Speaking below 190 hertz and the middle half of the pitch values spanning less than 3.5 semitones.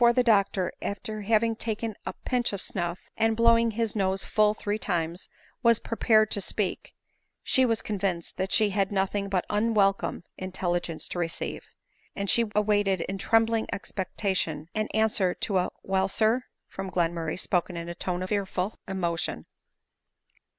No: high, 200 Hz; average, 2.9 semitones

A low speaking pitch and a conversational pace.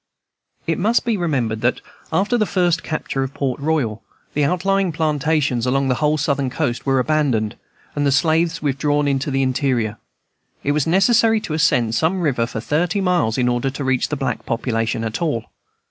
No: medium, 145 Hz; average, 180 wpm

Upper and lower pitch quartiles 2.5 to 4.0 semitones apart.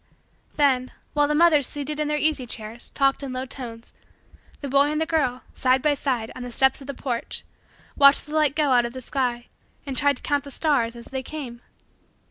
Yes: average, 2.8 semitones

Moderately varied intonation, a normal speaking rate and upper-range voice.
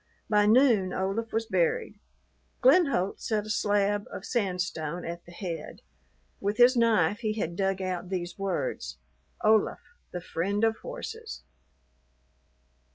No: average, 3.9 semitones; slow, 130 wpm; high, 205 Hz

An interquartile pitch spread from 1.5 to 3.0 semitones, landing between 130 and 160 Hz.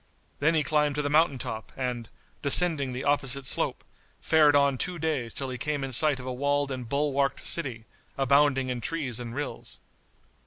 Yes: narrow, 2.6 semitones; medium, 140 Hz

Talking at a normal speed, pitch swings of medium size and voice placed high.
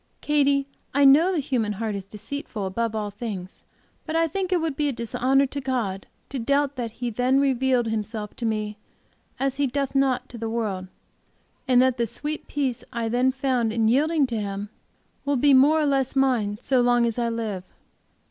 Yes: average, 195 wpm; average, 3.8 semitones; very high, 250 Hz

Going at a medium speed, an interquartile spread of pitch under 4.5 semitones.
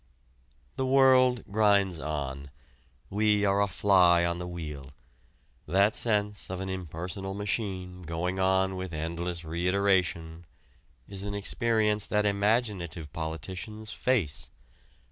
No: slow, 115 wpm; average, 3.3 semitones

